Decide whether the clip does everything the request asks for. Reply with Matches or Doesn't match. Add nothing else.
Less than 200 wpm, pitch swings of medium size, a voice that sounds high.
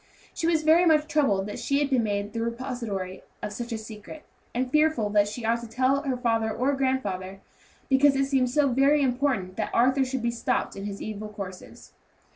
Doesn't match